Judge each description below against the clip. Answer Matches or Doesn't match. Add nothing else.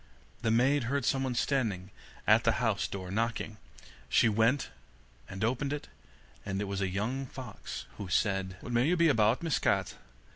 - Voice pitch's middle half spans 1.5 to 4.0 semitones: Doesn't match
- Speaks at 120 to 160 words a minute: Doesn't match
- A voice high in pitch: Doesn't match